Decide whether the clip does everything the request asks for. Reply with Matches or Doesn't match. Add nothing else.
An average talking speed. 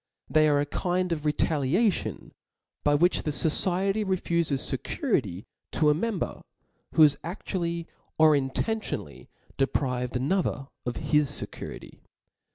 Doesn't match